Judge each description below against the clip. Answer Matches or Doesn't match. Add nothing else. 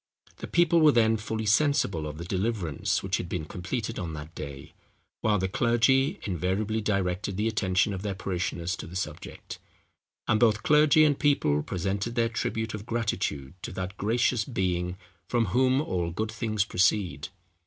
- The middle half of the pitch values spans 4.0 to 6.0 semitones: Matches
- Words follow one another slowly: Doesn't match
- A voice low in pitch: Matches